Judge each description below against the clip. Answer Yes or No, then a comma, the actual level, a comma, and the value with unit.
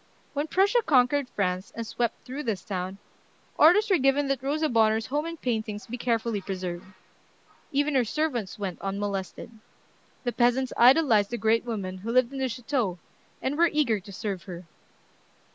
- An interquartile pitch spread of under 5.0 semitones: No, average, 5.3 semitones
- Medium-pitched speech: No, high, 235 Hz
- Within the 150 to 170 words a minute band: Yes, average, 165 wpm